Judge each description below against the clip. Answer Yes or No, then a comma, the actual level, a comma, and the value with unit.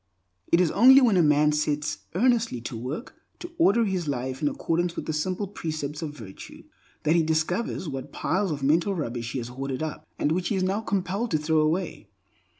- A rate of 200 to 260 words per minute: Yes, fast, 205 wpm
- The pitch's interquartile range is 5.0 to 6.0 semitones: No, average, 4.4 semitones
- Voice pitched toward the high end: No, medium, 160 Hz